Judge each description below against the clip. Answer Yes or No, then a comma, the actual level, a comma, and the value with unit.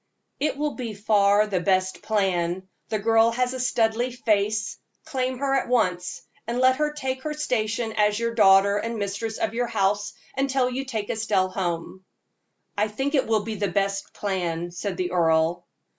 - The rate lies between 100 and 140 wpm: No, average, 175 wpm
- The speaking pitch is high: Yes, high, 215 Hz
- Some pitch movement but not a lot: Yes, average, 4.4 semitones